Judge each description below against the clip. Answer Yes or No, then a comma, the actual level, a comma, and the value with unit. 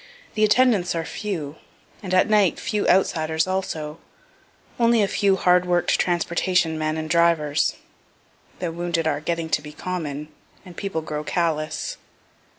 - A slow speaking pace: No, average, 145 wpm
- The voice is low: No, medium, 170 Hz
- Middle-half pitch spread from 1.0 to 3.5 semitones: Yes, average, 3.0 semitones